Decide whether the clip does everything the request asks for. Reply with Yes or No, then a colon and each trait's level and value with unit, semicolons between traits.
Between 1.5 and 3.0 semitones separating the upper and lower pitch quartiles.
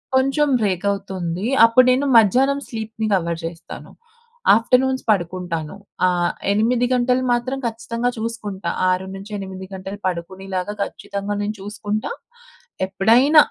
No: average, 4.2 semitones